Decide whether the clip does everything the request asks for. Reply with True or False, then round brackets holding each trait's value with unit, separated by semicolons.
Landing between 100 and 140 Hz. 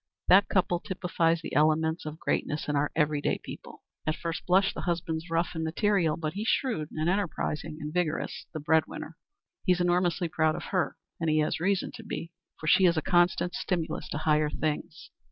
False (165 Hz)